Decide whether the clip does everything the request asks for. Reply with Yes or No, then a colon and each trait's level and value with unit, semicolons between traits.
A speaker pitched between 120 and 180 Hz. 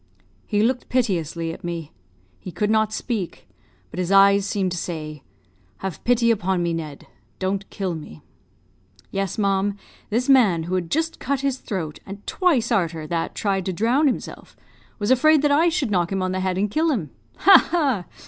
No: high, 195 Hz